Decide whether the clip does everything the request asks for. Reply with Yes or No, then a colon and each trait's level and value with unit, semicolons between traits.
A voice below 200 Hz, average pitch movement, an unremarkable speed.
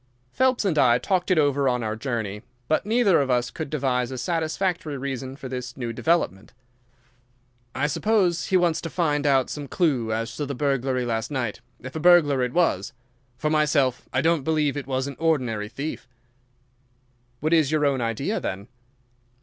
Yes: medium, 140 Hz; average, 4.2 semitones; average, 180 wpm